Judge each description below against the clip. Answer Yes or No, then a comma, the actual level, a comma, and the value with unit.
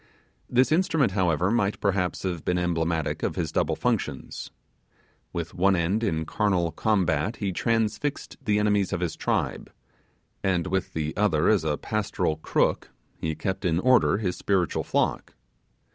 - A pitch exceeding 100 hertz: No, very low, 95 Hz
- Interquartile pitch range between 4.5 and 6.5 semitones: No, average, 3.8 semitones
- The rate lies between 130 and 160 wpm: Yes, average, 150 wpm